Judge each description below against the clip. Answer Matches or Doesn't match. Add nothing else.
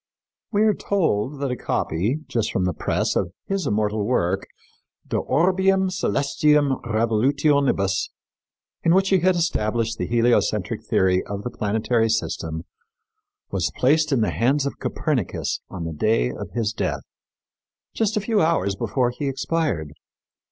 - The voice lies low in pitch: Matches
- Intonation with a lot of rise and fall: Matches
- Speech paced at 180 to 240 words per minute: Doesn't match